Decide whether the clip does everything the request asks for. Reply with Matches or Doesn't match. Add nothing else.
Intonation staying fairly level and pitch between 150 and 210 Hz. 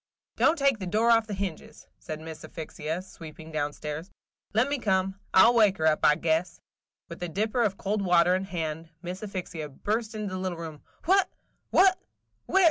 Doesn't match